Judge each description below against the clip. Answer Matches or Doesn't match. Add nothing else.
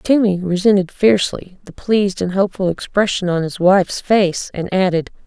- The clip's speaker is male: Doesn't match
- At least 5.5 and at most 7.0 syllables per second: Doesn't match